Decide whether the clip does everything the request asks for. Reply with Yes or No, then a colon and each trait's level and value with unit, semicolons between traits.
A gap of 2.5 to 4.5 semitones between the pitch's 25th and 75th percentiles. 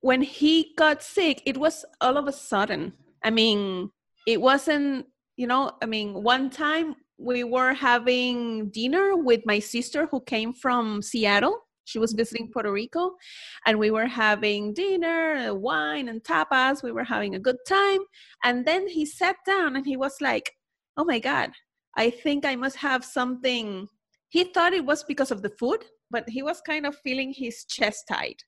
No: average, 5.0 semitones